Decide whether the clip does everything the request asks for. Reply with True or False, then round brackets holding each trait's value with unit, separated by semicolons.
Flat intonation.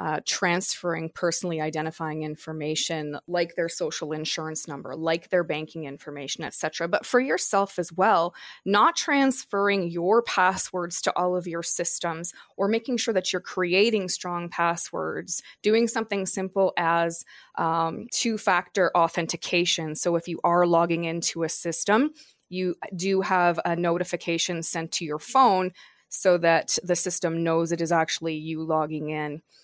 True (2.2 semitones)